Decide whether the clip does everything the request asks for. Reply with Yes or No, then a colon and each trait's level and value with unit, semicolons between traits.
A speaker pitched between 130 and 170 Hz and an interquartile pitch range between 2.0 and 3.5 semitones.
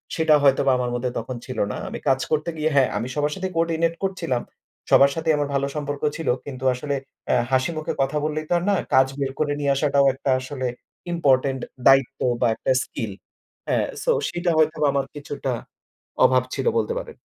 Yes: medium, 140 Hz; average, 2.9 semitones